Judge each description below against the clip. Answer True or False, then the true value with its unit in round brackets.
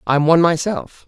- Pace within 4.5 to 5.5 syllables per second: True (5.4 syllables/s)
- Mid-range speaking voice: True (165 Hz)